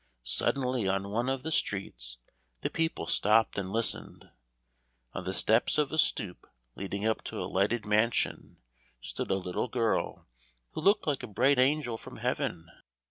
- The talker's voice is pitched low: Yes, low, 110 Hz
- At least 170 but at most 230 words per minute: No, average, 160 wpm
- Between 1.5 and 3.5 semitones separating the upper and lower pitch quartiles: No, average, 4.9 semitones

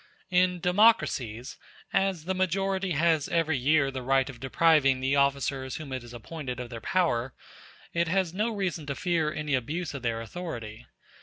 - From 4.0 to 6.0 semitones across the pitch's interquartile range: Yes, wide, 5.5 semitones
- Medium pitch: Yes, medium, 150 Hz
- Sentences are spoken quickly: No, average, 170 wpm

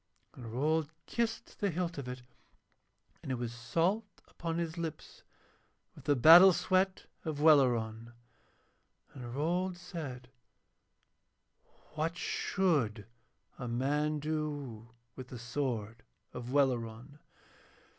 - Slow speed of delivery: Yes, slow, 110 wpm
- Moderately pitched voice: Yes, medium, 145 Hz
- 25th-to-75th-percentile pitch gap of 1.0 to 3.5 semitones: No, wide, 5.4 semitones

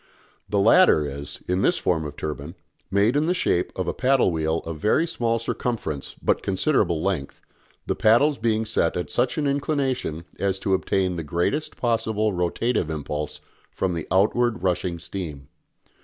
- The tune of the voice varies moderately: No, wide, 6.3 semitones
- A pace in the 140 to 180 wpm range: Yes, average, 165 wpm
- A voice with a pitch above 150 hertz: No, very low, 95 Hz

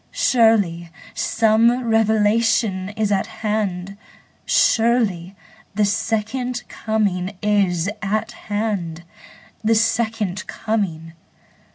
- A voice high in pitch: Yes, high, 215 Hz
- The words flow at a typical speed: No, slow, 80 wpm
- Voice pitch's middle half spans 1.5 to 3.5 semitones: Yes, average, 2.8 semitones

